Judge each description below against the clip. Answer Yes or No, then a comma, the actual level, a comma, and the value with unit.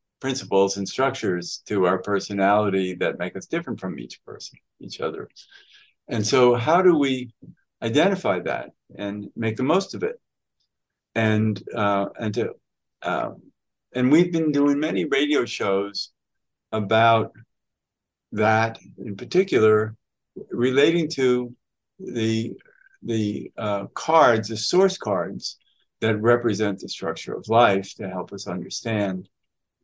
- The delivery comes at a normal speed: No, slow, 125 wpm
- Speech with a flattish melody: No, average, 3.8 semitones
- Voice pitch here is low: Yes, low, 110 Hz